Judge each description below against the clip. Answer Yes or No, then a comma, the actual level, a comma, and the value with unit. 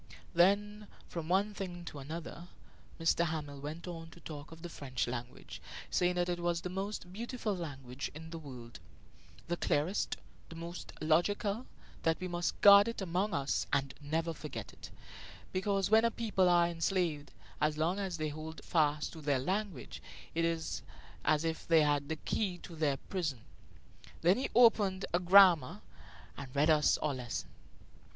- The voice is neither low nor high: Yes, medium, 170 Hz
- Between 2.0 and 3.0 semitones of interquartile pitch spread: No, average, 3.7 semitones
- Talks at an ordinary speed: Yes, average, 170 wpm